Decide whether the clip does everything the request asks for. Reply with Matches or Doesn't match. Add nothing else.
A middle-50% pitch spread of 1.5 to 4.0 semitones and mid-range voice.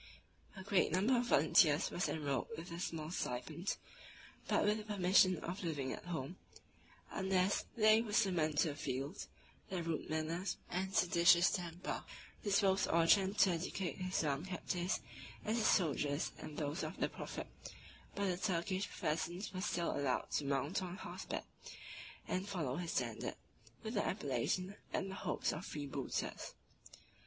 Matches